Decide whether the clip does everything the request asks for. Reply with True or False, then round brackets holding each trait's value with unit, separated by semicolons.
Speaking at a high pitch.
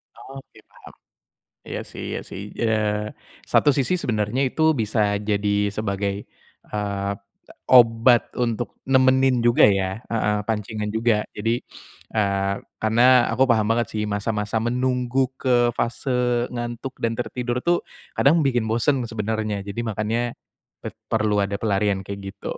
False (110 Hz)